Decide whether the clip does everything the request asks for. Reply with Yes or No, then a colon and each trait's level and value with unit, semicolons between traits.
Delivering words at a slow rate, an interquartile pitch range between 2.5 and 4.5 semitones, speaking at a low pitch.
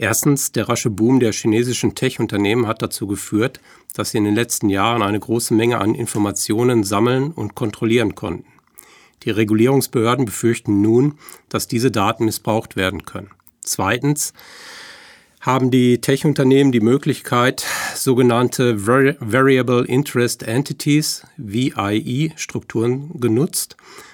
Yes: slow, 120 wpm; average, 2.9 semitones; low, 120 Hz